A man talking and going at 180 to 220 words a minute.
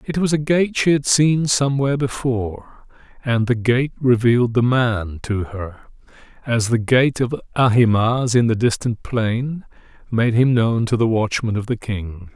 No: male; average, 170 wpm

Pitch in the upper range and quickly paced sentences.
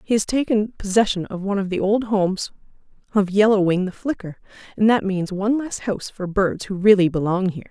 Yes: high, 200 Hz; fast, 210 wpm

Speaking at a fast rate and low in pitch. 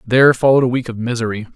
Yes: fast, 230 wpm; low, 120 Hz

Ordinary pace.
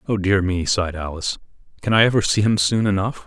No: fast, 220 wpm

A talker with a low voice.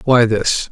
Yes: low, 115 Hz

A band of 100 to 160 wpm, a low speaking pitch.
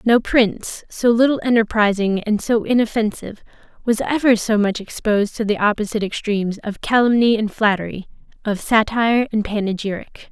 No: average, 145 wpm; high, 215 Hz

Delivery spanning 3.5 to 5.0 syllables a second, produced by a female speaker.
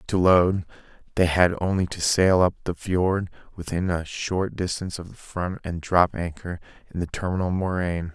No: 4.9 syllables/s; male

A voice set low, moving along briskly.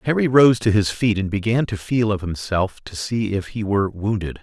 Yes: low, 105 Hz; fast, 230 wpm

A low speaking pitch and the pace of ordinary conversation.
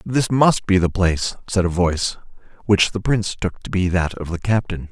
No: very low, 95 Hz; fast, 220 wpm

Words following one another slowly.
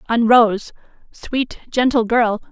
Yes: slow, 120 wpm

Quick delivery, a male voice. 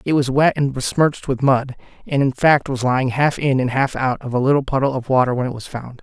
Yes: fast, 270 wpm; male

